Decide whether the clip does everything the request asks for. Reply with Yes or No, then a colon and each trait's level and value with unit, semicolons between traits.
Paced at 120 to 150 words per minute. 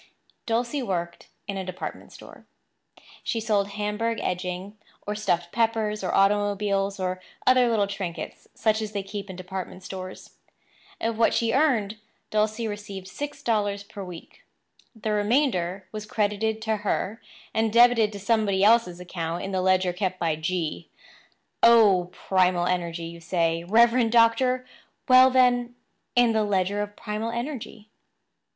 Yes: average, 145 wpm